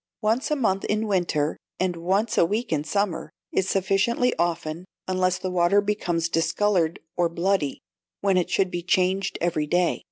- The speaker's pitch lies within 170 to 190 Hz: Yes, medium, 185 Hz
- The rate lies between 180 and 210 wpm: No, average, 165 wpm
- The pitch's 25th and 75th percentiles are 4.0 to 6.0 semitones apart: No, average, 2.9 semitones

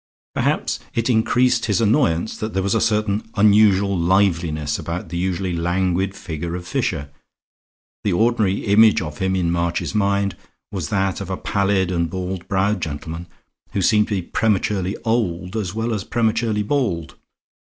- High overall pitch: No, very low, 95 Hz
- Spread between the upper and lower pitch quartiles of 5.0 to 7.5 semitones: No, average, 3.4 semitones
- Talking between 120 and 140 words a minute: No, average, 160 wpm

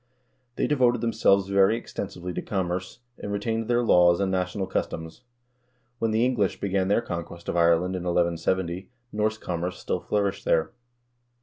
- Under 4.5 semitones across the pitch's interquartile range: Yes, average, 3.7 semitones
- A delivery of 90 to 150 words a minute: No, average, 160 wpm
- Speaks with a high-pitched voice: No, very low, 95 Hz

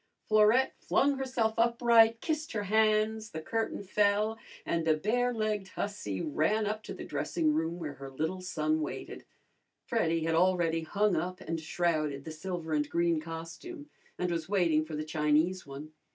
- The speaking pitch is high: No, medium, 180 Hz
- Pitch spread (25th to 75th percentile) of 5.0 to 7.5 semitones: Yes, wide, 5.4 semitones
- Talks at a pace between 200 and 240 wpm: No, average, 165 wpm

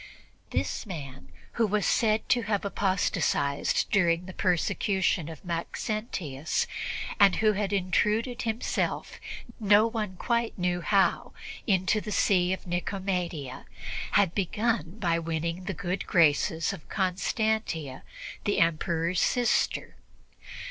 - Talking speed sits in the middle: No, slow, 115 wpm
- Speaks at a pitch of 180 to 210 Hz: Yes, medium, 185 Hz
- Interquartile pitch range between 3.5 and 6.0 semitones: Yes, average, 4.0 semitones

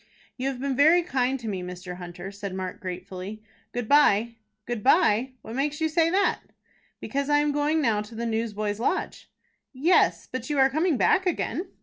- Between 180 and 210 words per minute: Yes, average, 190 wpm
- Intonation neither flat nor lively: No, wide, 6.1 semitones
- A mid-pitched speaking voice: No, very high, 250 Hz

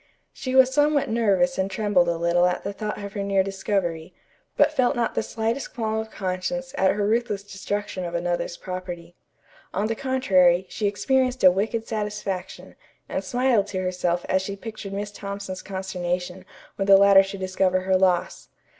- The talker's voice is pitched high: Yes, high, 195 Hz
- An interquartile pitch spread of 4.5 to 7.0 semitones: No, average, 3.1 semitones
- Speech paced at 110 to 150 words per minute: No, average, 175 wpm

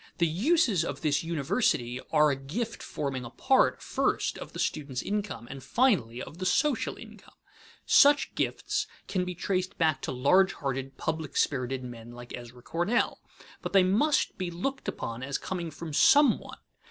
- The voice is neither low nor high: Yes, medium, 160 Hz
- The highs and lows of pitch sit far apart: Yes, wide, 6.5 semitones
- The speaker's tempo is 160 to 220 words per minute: Yes, average, 170 wpm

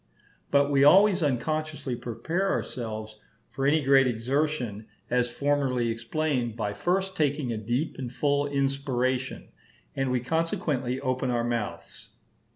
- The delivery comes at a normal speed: No, slow, 130 wpm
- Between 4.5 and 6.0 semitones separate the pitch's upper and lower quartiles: No, average, 3.4 semitones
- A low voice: Yes, low, 130 Hz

